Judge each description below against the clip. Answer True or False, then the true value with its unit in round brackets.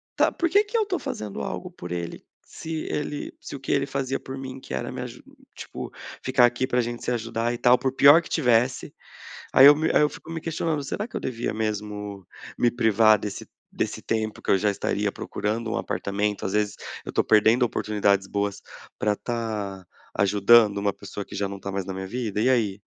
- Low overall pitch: True (115 Hz)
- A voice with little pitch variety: False (4.5 semitones)